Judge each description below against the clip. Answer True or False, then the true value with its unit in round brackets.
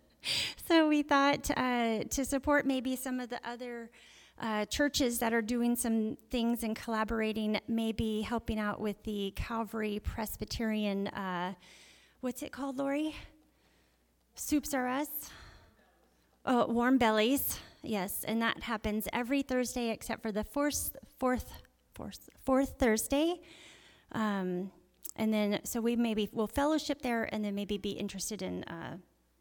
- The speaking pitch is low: False (230 Hz)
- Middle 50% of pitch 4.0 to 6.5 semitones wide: False (3.6 semitones)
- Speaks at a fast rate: False (140 wpm)